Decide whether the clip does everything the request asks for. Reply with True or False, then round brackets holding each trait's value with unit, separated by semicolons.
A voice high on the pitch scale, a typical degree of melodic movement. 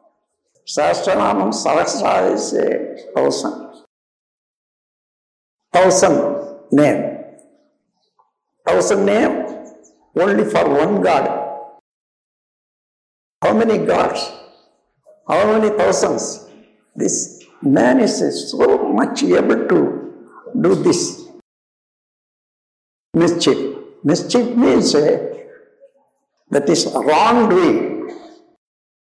False (340 Hz; 6.9 semitones)